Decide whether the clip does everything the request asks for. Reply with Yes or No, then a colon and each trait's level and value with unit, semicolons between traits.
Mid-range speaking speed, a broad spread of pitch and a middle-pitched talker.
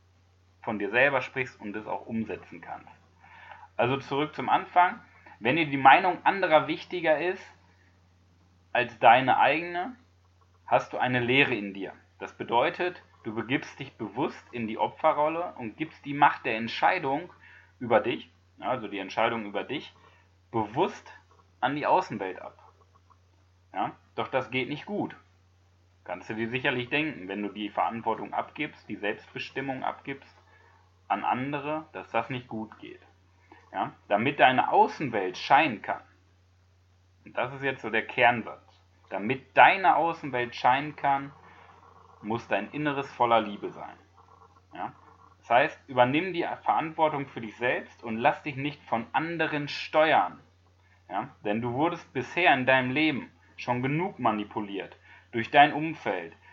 No: average, 145 wpm; wide, 7.6 semitones; low, 115 Hz